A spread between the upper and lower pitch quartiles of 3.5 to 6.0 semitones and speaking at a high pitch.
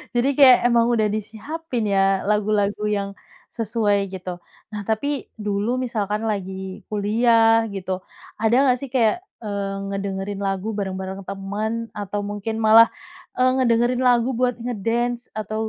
No: average, 2.9 semitones; high, 215 Hz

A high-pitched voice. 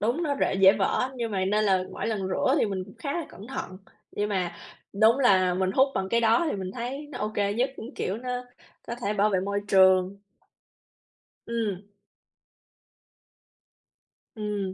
Yes: high, 205 Hz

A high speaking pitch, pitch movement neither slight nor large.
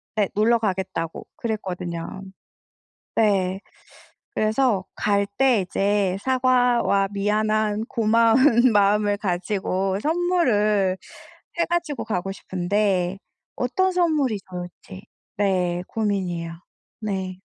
Yes: high, 205 Hz; average, 3.6 semitones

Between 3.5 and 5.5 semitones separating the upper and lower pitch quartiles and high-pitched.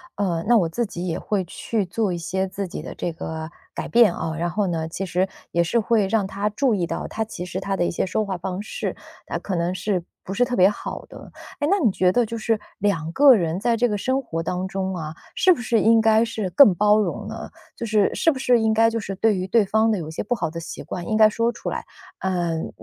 Yes: average, 4.1 semitones; high, 200 Hz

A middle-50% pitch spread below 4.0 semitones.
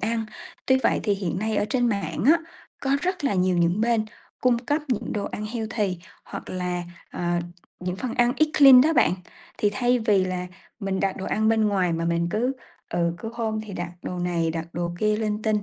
No: average, 4.5 semitones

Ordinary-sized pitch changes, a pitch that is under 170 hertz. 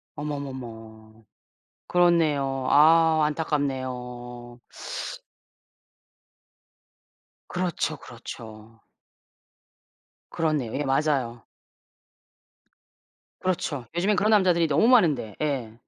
Yes: average, 5.0 semitones; medium, 140 Hz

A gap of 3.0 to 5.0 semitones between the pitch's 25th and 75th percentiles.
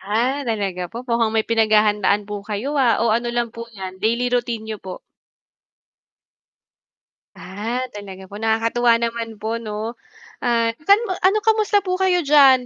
No: narrow, 2.6 semitones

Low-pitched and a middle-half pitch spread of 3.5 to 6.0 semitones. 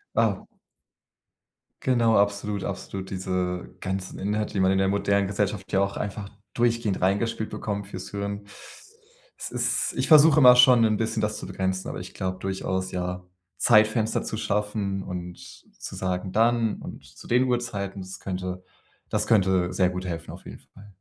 No: low, 100 Hz; narrow, 2.5 semitones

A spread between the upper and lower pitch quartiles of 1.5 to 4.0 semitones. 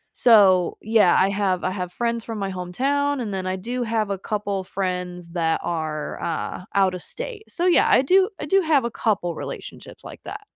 No: average, 5.1 semitones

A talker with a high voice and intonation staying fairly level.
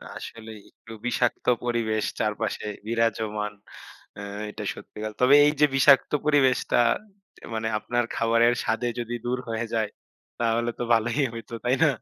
No: low, 115 Hz; narrow, 1.8 semitones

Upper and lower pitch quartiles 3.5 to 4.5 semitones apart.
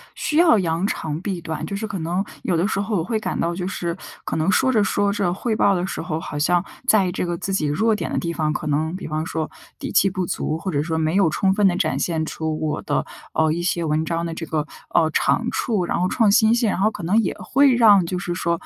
Yes: average, 3.9 semitones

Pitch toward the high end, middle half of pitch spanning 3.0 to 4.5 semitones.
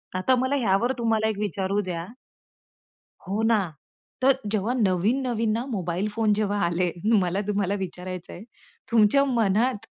Yes: high, 210 Hz; average, 3.6 semitones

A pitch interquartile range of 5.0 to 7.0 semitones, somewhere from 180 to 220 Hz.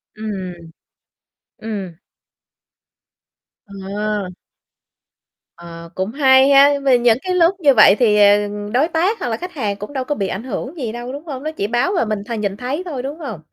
No: wide, 5.6 semitones; high, 240 Hz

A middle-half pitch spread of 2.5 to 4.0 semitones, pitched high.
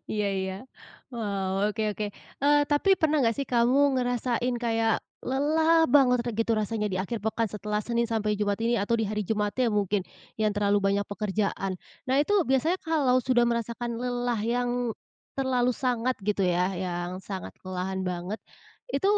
Yes: average, 3.5 semitones; high, 230 Hz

